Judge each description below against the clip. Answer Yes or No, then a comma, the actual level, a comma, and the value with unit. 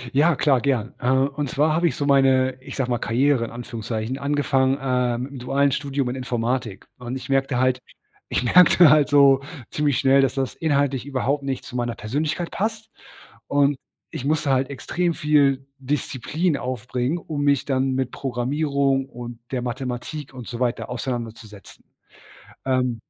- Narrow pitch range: Yes, narrow, 2.3 semitones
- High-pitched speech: No, low, 135 Hz